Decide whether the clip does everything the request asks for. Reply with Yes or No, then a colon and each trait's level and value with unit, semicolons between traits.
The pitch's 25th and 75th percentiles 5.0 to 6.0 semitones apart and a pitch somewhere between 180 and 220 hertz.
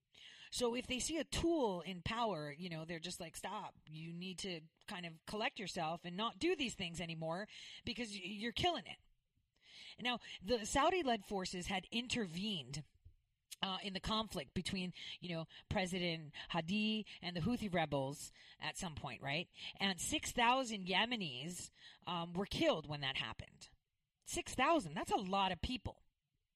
Yes: wide, 5.5 semitones; high, 190 Hz